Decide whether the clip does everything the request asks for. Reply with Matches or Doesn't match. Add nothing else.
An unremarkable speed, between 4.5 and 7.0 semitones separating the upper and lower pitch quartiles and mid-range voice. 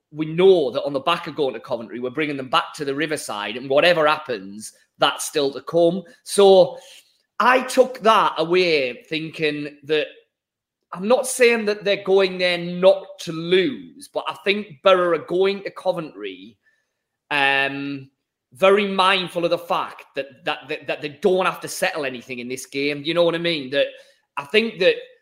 Matches